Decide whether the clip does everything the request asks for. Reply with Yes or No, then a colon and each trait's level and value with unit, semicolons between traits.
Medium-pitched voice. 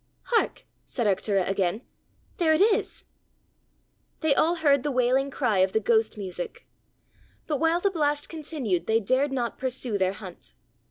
No: very high, 255 Hz